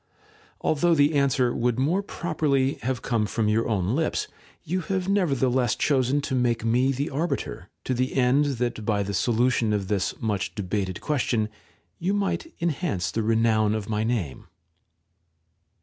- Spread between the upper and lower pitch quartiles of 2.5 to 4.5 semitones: No, average, 4.9 semitones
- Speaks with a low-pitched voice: Yes, low, 125 Hz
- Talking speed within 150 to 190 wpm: Yes, average, 160 wpm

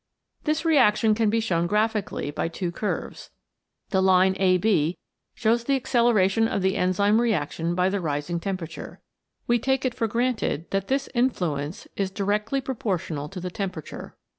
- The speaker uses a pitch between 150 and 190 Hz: No, high, 200 Hz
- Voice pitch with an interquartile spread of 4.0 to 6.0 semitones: Yes, average, 4.3 semitones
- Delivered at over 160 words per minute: No, average, 155 wpm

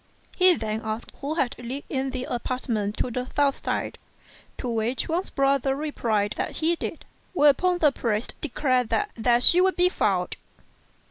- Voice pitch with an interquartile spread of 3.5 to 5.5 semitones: Yes, average, 4.7 semitones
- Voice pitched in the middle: No, very high, 260 Hz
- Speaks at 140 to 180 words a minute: Yes, average, 160 wpm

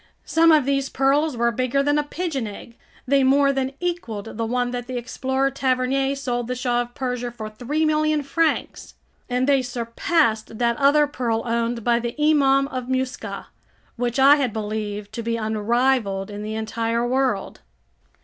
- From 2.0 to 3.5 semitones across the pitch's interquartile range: Yes, average, 3.0 semitones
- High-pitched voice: Yes, very high, 250 Hz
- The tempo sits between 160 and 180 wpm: Yes, average, 170 wpm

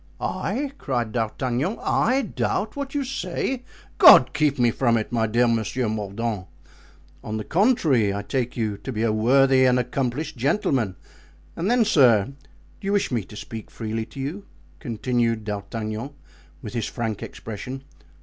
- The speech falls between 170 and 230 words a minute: No, average, 160 wpm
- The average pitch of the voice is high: No, low, 120 Hz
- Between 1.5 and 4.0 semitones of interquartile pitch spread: No, average, 4.4 semitones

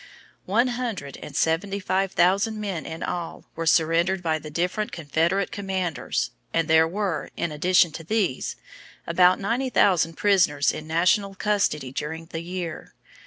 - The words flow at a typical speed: Yes, average, 155 wpm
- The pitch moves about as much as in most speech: Yes, average, 3.4 semitones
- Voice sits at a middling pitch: Yes, medium, 175 Hz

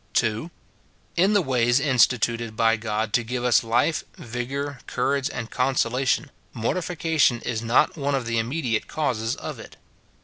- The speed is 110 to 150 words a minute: Yes, average, 145 wpm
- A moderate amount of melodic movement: Yes, average, 3.5 semitones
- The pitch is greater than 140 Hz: No, low, 125 Hz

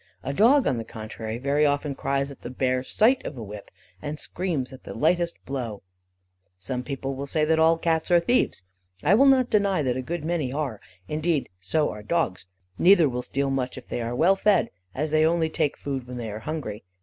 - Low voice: No, medium, 145 Hz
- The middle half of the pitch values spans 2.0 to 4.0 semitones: No, average, 4.9 semitones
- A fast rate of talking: Yes, fast, 210 wpm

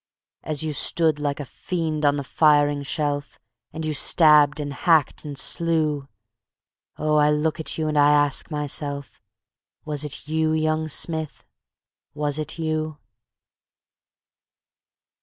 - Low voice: No, medium, 150 Hz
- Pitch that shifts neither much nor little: No, narrow, 1.4 semitones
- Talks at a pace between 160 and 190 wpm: No, slow, 135 wpm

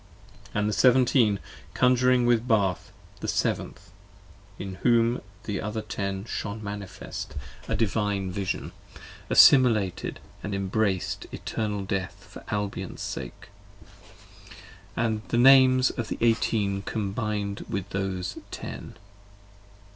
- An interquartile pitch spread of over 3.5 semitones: No, average, 3.1 semitones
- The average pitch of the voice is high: No, low, 105 Hz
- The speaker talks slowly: Yes, slow, 115 wpm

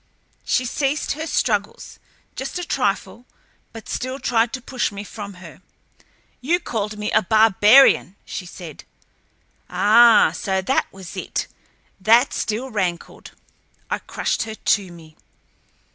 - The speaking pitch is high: Yes, high, 220 Hz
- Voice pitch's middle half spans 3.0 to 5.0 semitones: Yes, average, 4.7 semitones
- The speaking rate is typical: No, slow, 130 wpm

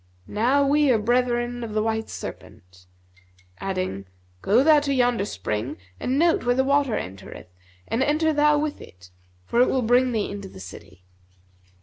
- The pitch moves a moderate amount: No, wide, 6.3 semitones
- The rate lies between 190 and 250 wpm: No, average, 165 wpm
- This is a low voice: No, high, 240 Hz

